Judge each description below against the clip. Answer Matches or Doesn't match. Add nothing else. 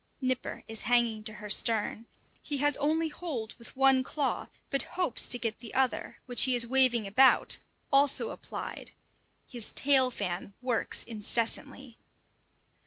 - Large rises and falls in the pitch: Doesn't match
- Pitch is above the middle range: Matches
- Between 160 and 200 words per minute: Doesn't match